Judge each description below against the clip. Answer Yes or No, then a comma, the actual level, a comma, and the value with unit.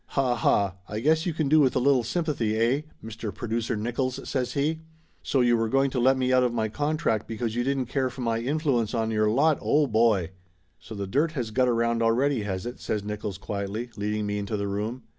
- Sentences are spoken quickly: Yes, fast, 230 wpm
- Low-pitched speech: Yes, low, 120 Hz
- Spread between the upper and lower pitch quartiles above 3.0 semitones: Yes, average, 3.8 semitones